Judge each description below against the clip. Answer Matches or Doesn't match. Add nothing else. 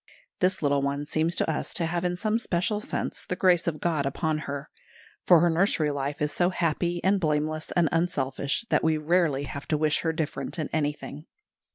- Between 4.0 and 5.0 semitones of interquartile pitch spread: Doesn't match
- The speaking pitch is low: Doesn't match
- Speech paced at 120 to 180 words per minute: Doesn't match